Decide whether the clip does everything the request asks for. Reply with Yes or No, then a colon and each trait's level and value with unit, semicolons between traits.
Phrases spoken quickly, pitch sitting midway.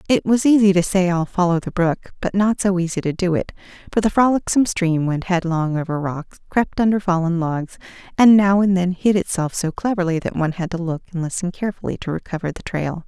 Yes: fast, 220 wpm; medium, 180 Hz